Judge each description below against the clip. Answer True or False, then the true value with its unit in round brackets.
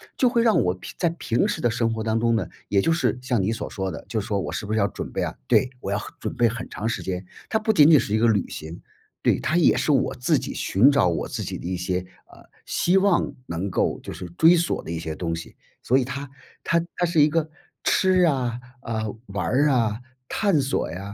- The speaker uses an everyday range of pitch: False (7.6 semitones)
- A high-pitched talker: False (115 Hz)